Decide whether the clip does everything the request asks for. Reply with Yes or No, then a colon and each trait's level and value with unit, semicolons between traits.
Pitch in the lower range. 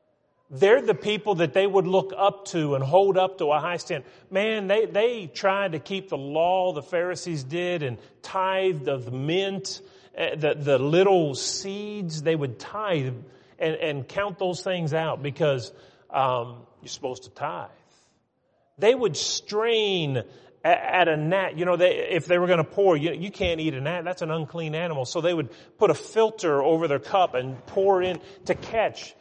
No: medium, 175 Hz